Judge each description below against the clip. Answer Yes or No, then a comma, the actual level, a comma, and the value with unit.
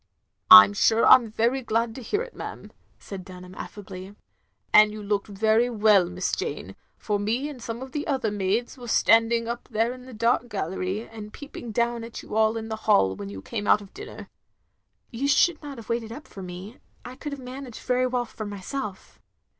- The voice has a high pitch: Yes, high, 225 Hz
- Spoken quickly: Yes, fast, 210 wpm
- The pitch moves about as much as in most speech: Yes, average, 3.3 semitones